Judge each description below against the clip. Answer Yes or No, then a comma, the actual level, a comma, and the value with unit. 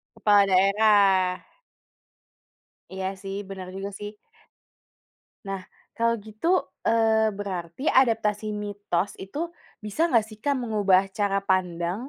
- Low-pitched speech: No, high, 205 Hz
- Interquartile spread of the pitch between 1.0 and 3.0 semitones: Yes, narrow, 2.4 semitones